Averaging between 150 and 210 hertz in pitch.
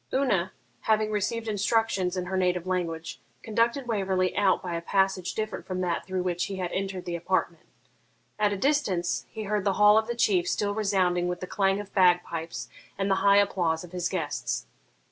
Yes: high, 190 Hz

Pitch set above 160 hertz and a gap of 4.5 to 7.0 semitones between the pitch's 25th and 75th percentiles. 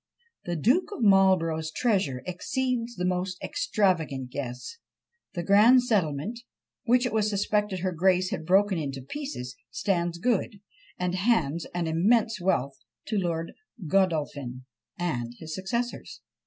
Yes: medium, 185 Hz; average, 5.1 semitones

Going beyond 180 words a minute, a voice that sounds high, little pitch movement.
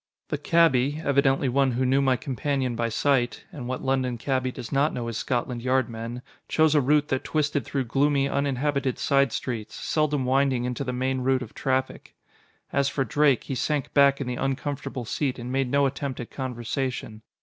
No: average, 190 wpm; low, 130 Hz; narrow, 2.0 semitones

